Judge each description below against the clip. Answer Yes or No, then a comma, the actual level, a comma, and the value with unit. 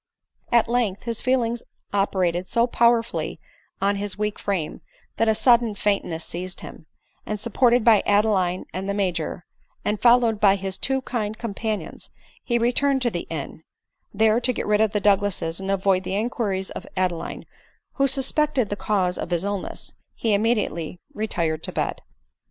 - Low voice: No, high, 205 Hz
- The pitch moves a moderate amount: Yes, average, 3.8 semitones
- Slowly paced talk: No, average, 170 wpm